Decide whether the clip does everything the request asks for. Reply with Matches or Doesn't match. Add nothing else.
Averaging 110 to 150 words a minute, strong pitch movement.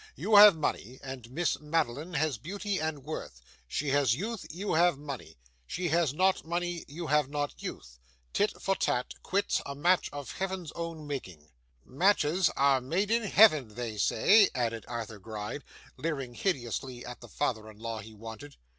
Doesn't match